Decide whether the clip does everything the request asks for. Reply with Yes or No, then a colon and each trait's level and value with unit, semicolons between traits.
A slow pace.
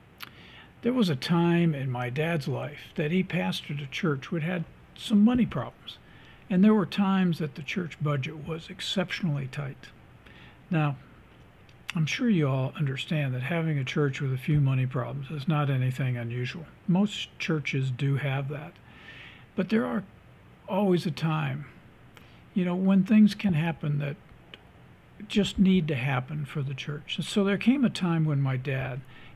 No: average, 165 wpm